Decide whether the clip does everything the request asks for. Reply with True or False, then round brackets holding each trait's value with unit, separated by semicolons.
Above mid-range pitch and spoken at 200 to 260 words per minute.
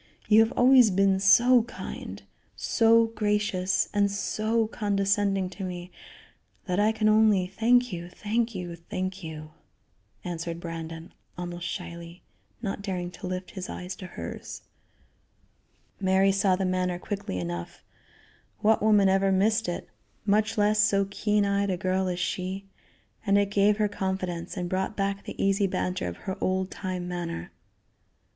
False (195 Hz; 150 wpm)